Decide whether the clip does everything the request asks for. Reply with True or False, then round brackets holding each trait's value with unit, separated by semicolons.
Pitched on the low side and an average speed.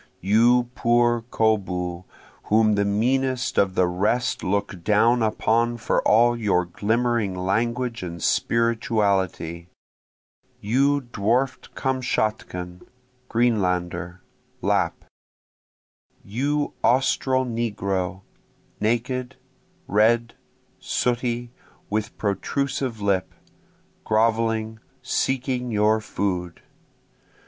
False (110 Hz; 80 wpm)